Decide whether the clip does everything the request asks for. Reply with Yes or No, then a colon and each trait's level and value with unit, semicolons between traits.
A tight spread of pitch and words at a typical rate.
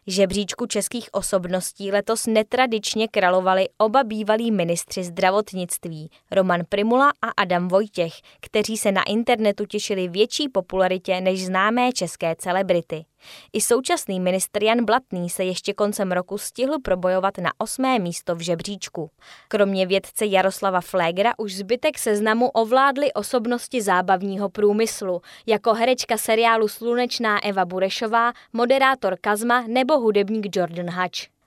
No: average, 3.6 semitones; average, 125 wpm